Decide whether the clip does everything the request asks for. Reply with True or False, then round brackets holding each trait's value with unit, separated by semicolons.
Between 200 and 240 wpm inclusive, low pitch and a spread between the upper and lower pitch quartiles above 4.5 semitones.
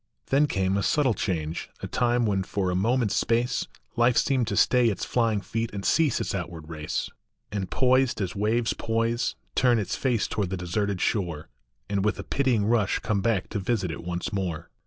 False (205 wpm; 105 Hz; 4.0 semitones)